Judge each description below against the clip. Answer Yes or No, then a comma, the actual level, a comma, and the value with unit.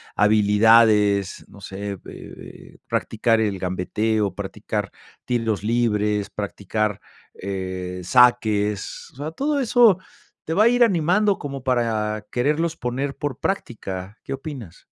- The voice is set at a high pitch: No, low, 110 Hz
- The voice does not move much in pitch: No, wide, 5.6 semitones